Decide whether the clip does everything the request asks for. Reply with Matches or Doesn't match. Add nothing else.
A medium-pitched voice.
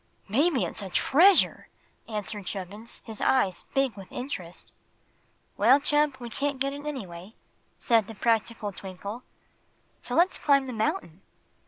Doesn't match